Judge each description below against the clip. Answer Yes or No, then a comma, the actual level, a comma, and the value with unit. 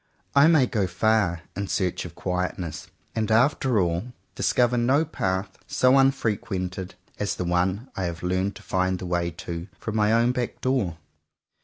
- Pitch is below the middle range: Yes, low, 100 Hz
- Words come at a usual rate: Yes, average, 165 wpm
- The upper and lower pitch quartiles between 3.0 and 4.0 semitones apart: No, average, 5.1 semitones